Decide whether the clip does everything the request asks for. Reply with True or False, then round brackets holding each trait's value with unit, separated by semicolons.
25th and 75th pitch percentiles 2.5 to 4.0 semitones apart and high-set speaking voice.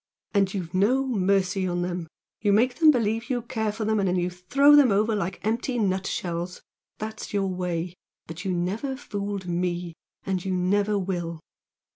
True (3.4 semitones; 195 Hz)